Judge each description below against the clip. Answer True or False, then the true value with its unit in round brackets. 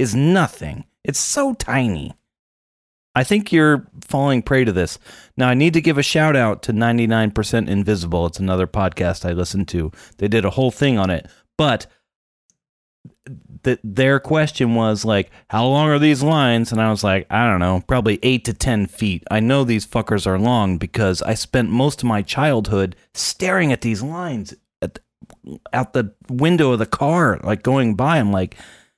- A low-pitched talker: True (115 Hz)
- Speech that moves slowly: False (185 wpm)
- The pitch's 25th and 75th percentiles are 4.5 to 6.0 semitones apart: True (5.3 semitones)